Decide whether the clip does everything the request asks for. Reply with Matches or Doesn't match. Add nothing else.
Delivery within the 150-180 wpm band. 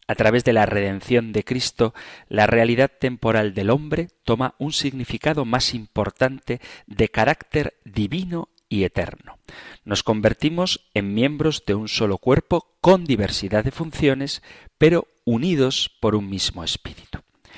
Doesn't match